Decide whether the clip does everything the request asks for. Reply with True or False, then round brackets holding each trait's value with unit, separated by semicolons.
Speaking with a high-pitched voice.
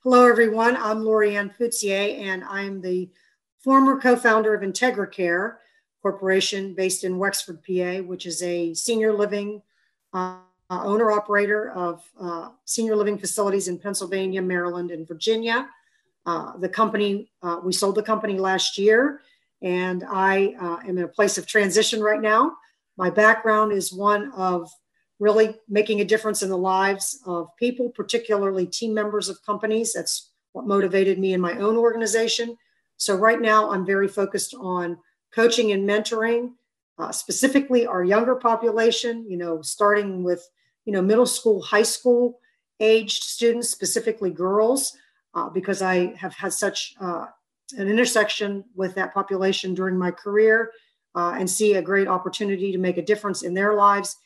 True (205 Hz)